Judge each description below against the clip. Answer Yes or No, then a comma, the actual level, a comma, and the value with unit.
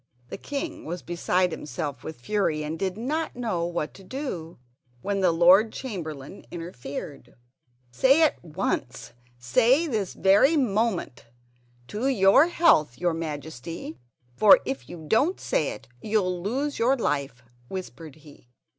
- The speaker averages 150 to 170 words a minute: No, slow, 135 wpm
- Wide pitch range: Yes, wide, 6.8 semitones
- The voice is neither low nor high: Yes, medium, 180 Hz